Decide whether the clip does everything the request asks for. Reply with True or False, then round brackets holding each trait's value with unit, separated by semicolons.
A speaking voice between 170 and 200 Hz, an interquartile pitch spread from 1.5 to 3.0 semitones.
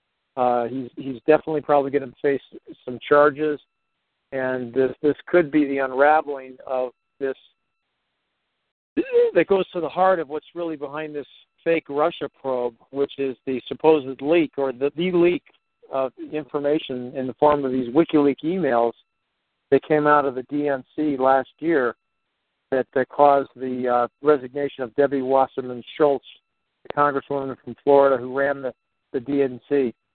False (140 Hz; 2.6 semitones)